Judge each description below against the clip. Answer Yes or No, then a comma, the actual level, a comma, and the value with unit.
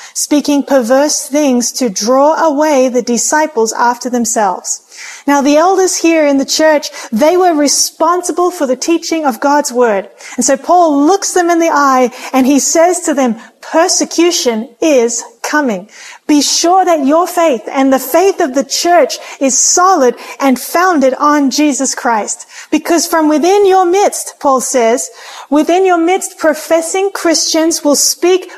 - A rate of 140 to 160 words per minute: Yes, average, 155 wpm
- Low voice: No, very high, 300 Hz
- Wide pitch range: No, average, 4.2 semitones